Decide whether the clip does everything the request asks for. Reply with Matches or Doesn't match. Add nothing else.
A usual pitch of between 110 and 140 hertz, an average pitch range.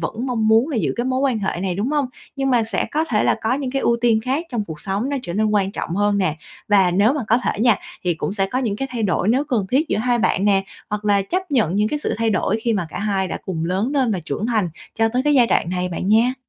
Doesn't match